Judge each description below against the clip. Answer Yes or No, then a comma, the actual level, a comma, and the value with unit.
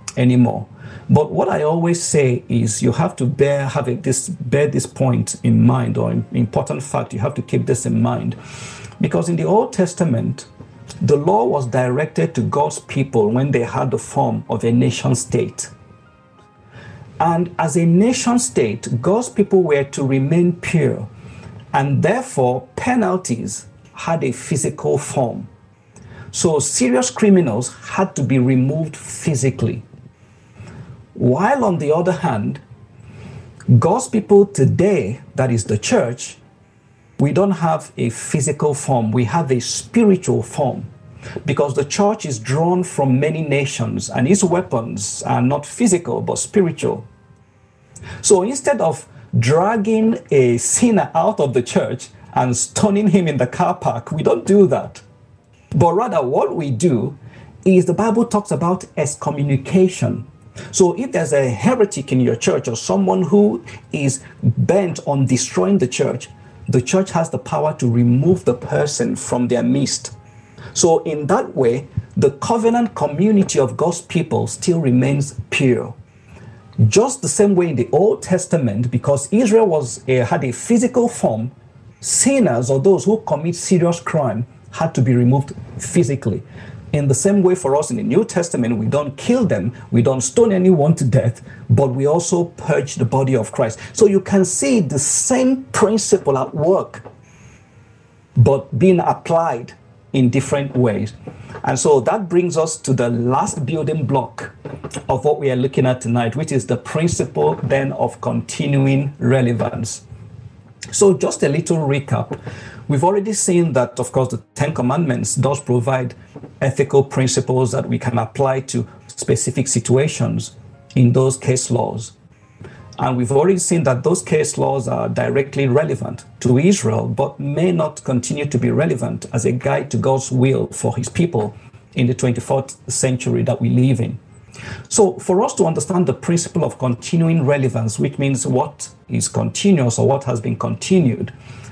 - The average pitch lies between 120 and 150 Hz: Yes, low, 135 Hz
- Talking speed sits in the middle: Yes, average, 155 wpm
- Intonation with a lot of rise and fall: Yes, wide, 5.8 semitones